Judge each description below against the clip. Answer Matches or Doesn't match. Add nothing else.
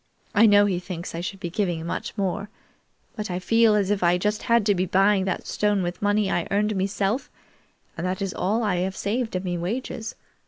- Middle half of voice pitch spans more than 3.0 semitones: Doesn't match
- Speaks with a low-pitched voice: Doesn't match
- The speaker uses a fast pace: Matches